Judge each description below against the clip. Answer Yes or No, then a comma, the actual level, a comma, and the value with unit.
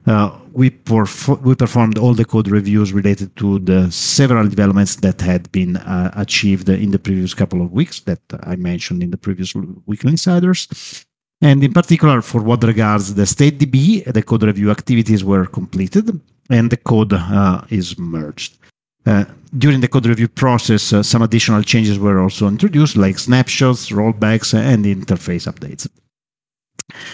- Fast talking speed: No, average, 160 wpm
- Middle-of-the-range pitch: No, low, 110 Hz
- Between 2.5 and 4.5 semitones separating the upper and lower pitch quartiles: No, average, 4.9 semitones